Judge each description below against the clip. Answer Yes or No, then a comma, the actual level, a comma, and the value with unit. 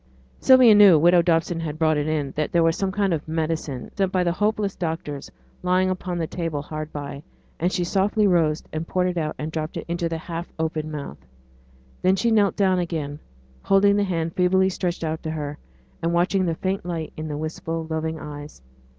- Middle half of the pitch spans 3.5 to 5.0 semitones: No, average, 2.9 semitones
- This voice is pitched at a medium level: Yes, medium, 165 Hz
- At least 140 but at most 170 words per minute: No, fast, 205 wpm